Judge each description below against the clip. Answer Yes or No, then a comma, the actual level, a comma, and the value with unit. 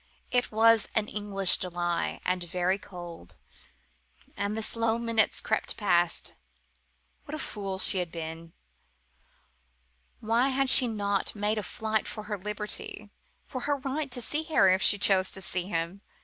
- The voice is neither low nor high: No, high, 205 Hz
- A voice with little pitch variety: No, average, 3.8 semitones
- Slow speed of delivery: No, average, 155 wpm